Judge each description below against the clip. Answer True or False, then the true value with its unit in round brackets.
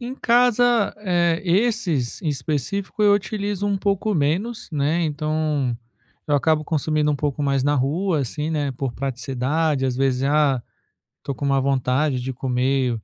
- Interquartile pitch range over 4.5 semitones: True (5.4 semitones)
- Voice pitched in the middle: True (150 Hz)